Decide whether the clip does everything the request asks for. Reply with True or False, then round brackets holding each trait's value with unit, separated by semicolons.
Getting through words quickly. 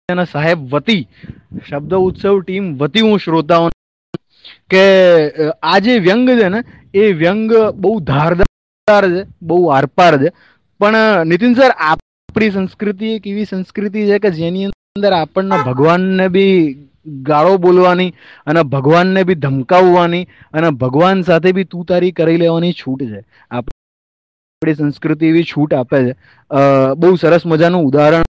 False (70 wpm)